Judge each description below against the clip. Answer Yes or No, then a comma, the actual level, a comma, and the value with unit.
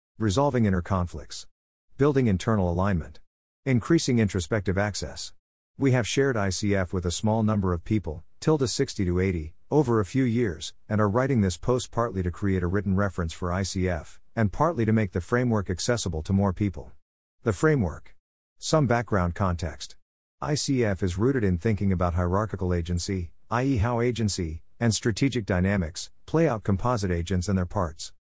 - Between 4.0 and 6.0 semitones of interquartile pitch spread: Yes, average, 4.8 semitones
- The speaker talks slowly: No, average, 160 wpm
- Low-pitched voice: Yes, low, 100 Hz